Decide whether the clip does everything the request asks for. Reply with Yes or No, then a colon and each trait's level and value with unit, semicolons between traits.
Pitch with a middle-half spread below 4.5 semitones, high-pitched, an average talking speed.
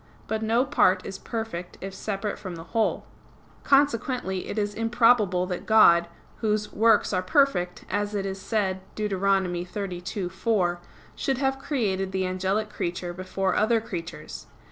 Yes: average, 3.2 semitones; high, 195 Hz; average, 145 wpm